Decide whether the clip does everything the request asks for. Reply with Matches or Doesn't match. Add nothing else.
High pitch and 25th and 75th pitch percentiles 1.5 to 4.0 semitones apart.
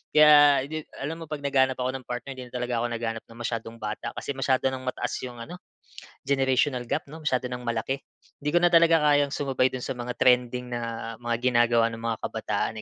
Doesn't match